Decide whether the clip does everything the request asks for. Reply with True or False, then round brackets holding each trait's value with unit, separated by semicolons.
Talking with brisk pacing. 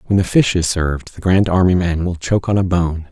True (270 wpm)